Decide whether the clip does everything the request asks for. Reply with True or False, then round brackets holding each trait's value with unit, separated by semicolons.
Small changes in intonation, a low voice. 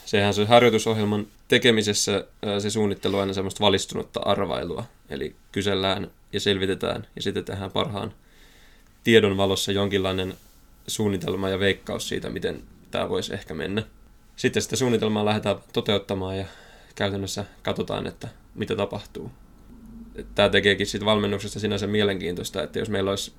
True (1.6 semitones; 100 Hz)